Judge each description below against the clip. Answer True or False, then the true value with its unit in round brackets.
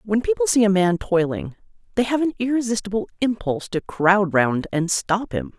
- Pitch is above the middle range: True (205 Hz)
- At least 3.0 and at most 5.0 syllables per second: False (5.2 syllables/s)